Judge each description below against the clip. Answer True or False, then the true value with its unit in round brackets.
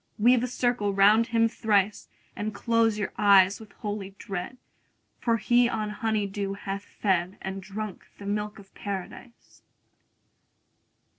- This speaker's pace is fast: False (145 wpm)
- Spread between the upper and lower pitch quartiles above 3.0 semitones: False (2.4 semitones)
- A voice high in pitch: True (210 Hz)